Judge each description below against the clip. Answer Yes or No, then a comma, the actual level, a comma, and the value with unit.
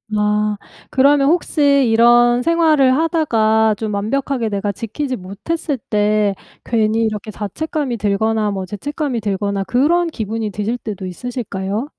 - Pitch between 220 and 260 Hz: Yes, high, 225 Hz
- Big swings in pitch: No, average, 4.8 semitones